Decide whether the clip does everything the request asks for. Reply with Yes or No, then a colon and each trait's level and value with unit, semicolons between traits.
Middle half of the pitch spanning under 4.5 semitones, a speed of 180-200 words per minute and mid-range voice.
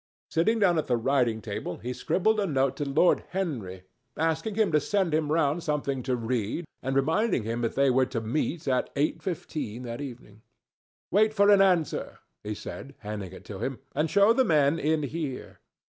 No: wide, 5.5 semitones; average, 190 wpm; medium, 145 Hz